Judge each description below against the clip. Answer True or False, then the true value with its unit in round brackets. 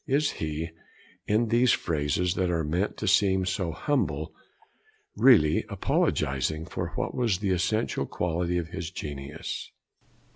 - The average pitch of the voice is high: False (90 Hz)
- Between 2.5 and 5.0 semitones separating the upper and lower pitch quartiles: True (4.2 semitones)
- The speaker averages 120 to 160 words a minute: True (135 wpm)